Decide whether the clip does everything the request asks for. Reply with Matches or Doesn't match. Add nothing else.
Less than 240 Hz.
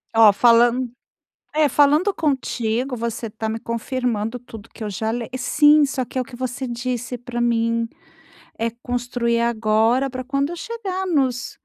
Doesn't match